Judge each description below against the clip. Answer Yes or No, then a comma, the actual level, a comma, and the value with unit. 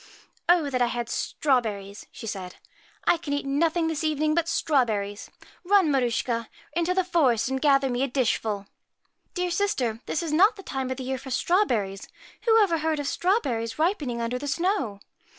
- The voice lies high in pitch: Yes, very high, 275 Hz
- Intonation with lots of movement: Yes, wide, 6.1 semitones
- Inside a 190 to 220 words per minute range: Yes, average, 200 wpm